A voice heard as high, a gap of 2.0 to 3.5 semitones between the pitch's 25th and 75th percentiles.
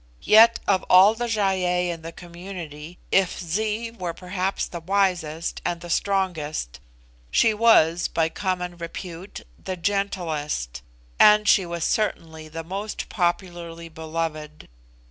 No: medium, 175 Hz; average, 3.2 semitones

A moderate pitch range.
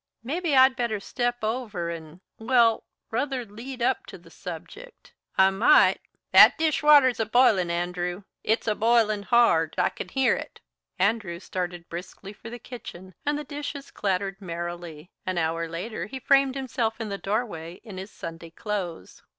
No: wide, 5.8 semitones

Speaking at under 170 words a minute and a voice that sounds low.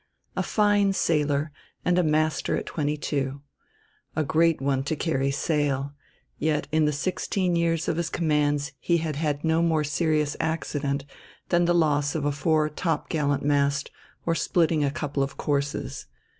No: average, 160 wpm; medium, 150 Hz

